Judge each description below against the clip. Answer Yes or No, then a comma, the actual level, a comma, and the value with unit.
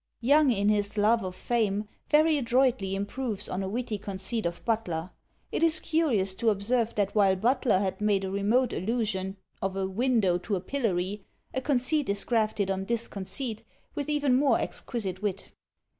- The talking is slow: No, average, 175 wpm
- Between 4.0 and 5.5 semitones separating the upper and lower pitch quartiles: Yes, average, 4.3 semitones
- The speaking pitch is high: Yes, high, 215 Hz